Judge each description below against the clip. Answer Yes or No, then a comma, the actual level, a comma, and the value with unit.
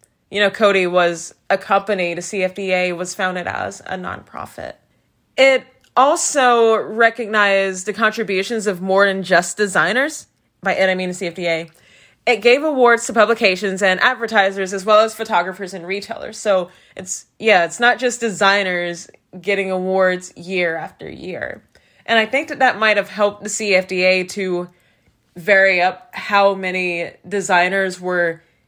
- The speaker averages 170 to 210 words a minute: No, average, 150 wpm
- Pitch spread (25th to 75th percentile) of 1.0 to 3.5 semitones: Yes, average, 3.0 semitones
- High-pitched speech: Yes, high, 195 Hz